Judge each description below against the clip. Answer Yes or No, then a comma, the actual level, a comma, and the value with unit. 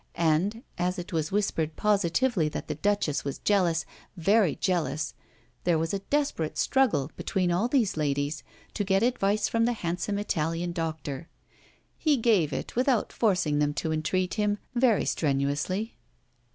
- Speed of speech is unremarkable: Yes, average, 150 wpm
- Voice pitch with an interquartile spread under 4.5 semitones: No, average, 5.0 semitones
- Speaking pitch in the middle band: Yes, medium, 180 Hz